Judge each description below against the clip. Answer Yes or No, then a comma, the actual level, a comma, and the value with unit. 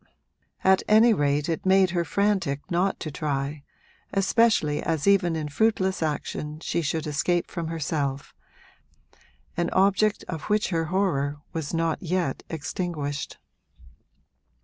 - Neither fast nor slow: No, slow, 125 wpm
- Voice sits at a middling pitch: Yes, medium, 165 Hz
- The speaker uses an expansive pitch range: No, average, 4.3 semitones